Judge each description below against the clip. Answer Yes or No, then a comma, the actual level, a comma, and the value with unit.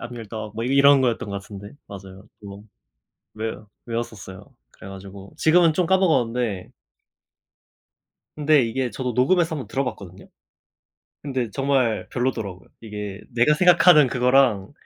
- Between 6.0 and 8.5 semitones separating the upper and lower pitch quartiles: No, average, 5.3 semitones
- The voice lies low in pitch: Yes, low, 120 Hz